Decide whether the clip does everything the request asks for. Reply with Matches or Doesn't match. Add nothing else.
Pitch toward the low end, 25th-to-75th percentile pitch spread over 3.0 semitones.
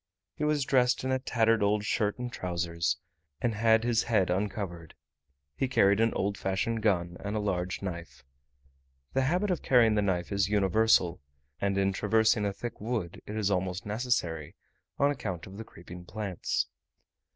Matches